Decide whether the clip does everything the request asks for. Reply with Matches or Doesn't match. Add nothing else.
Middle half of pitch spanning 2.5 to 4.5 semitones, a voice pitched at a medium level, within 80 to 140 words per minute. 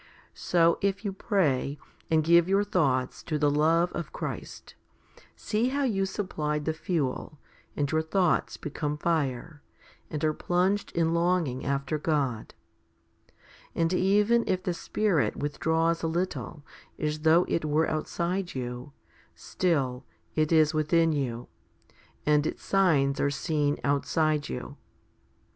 Matches